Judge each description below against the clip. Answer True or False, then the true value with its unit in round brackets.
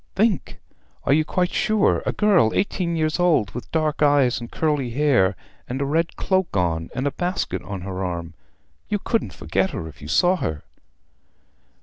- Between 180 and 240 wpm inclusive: True (185 wpm)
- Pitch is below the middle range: False (145 Hz)